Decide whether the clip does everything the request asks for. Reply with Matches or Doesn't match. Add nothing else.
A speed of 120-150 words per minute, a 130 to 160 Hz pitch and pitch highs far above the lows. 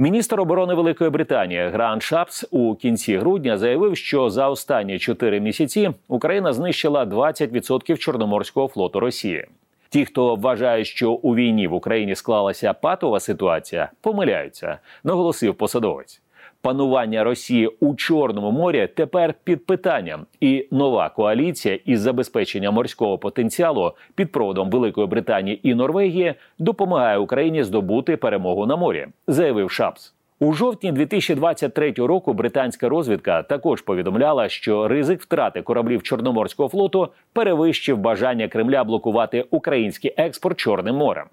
Matches